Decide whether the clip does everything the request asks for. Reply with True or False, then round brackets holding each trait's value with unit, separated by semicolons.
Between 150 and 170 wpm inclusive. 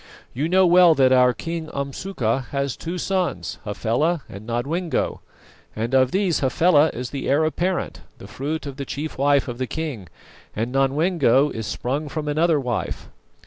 True (165 wpm)